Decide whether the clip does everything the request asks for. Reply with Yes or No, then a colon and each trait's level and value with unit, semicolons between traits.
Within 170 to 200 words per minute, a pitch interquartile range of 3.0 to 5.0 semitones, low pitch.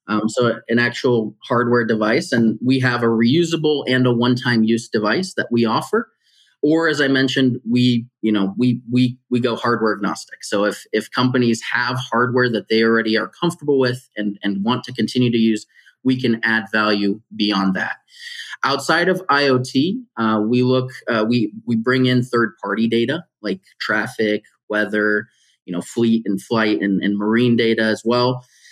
No: average, 180 wpm; narrow, 2.5 semitones; low, 120 Hz